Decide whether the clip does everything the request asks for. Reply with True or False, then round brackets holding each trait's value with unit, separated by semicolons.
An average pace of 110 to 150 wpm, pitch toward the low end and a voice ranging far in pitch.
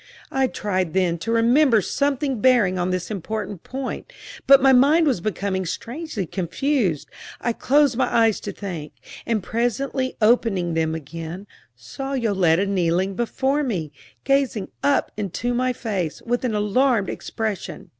False (145 wpm; 220 Hz; 5.9 semitones)